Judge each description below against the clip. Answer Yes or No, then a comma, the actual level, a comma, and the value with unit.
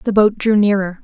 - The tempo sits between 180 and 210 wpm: No, fast, 230 wpm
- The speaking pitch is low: No, high, 205 Hz